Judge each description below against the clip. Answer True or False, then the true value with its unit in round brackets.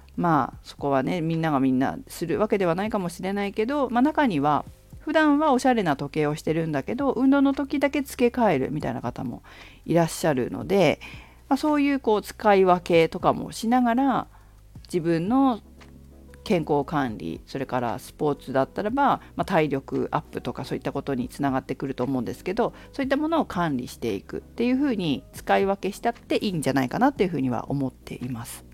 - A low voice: False (165 Hz)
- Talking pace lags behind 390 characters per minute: False (420 characters per minute)